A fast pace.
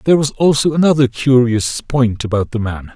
No: average, 185 wpm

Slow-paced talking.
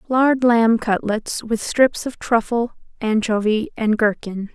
Yes: slow, 130 wpm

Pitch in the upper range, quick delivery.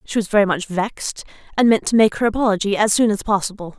Yes: high, 205 Hz; fast, 240 wpm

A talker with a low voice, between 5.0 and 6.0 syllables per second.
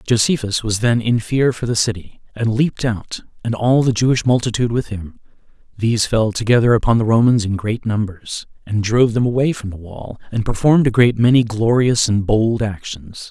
Yes: low, 115 Hz; 5.4 syllables/s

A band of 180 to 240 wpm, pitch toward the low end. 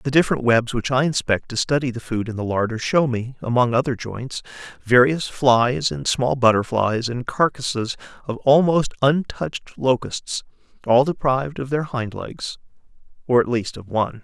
No: average, 170 wpm; low, 125 Hz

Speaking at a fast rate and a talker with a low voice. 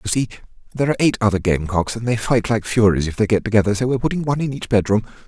Yes: fast, 260 wpm; low, 110 Hz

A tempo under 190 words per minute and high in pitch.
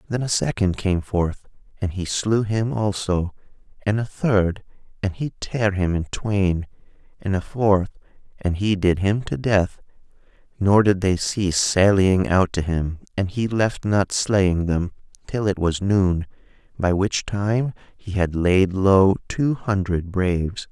No: average, 160 wpm; low, 100 Hz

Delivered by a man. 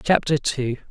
Yes: male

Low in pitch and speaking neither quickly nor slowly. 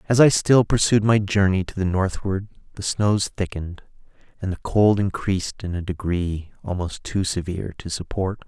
Yes: very low, 95 Hz; average, 170 wpm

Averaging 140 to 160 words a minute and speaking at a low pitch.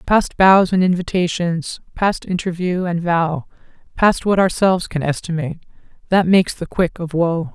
No: average, 150 wpm; medium, 180 Hz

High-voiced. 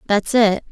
Yes: high, 210 Hz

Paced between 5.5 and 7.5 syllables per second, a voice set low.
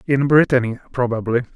Yes: 6.0 syllables/s; low, 125 Hz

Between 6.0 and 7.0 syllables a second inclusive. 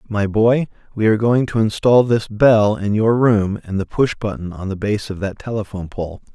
No: 5.0 syllables/s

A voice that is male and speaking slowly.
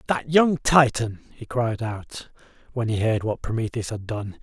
No: male; average, 175 wpm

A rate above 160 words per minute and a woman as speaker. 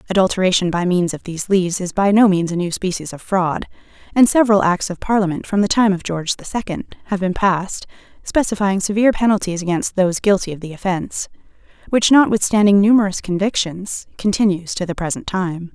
Yes: average, 185 wpm; female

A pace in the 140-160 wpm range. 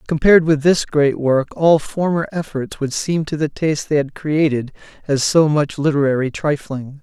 No: average, 180 wpm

